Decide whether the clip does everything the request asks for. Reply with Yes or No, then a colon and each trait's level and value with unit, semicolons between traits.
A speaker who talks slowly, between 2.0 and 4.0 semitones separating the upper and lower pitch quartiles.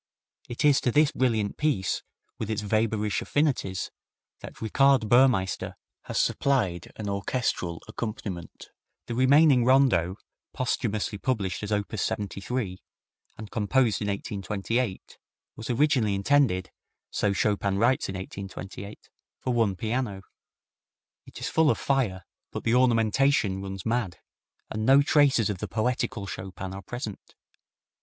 No: slow, 130 wpm; average, 4.6 semitones